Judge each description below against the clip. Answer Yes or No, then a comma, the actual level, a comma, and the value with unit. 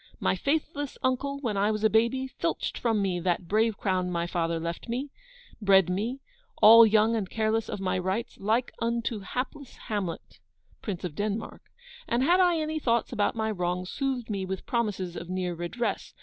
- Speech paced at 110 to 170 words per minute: No, average, 180 wpm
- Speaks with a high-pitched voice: Yes, high, 215 Hz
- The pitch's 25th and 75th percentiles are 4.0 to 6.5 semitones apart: Yes, average, 4.4 semitones